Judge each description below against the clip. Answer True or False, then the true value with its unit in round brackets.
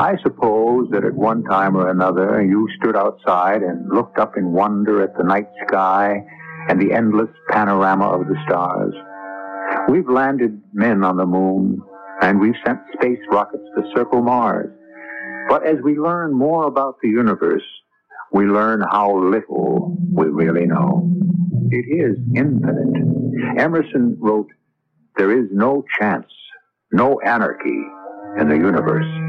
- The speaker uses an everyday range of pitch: False (5.9 semitones)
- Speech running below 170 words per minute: True (145 wpm)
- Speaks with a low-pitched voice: True (105 Hz)